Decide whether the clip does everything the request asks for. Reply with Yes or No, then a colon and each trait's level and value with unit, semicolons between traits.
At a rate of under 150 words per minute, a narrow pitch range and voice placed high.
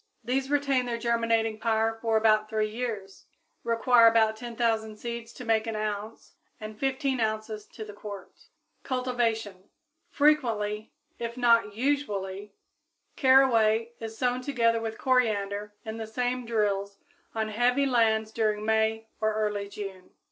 Yes: slow, 135 wpm; narrow, 2.1 semitones; high, 225 Hz